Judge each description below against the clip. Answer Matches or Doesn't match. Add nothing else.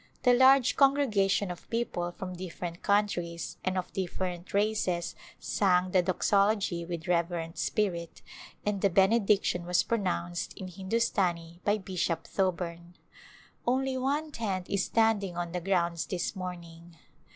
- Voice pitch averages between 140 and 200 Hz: Matches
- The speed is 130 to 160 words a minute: Matches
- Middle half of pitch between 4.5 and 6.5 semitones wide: Doesn't match